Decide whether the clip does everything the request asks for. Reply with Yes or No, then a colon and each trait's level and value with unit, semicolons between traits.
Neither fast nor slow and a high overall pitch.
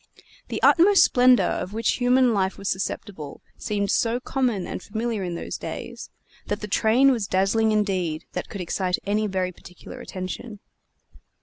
Yes: average, 160 wpm; high, 205 Hz